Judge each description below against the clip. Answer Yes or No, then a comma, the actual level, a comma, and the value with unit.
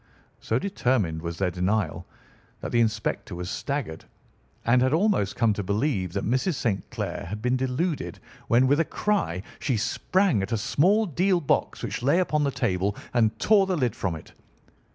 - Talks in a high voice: No, low, 120 Hz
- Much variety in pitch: Yes, wide, 7.3 semitones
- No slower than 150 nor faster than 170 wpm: No, average, 180 wpm